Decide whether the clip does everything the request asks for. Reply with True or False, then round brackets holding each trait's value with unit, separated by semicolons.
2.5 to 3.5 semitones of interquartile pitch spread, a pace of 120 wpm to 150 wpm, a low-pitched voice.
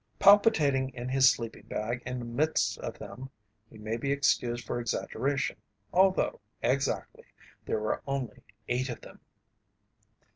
True (2.8 semitones; 140 wpm; 125 Hz)